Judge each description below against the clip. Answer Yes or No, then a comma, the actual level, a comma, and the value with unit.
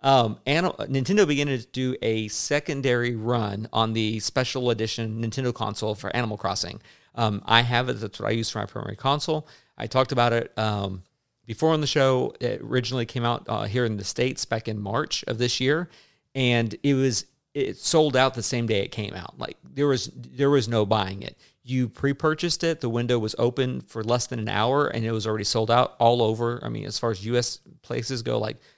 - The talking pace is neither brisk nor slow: No, fast, 215 wpm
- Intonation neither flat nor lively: Yes, average, 3.2 semitones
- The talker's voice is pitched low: Yes, low, 120 Hz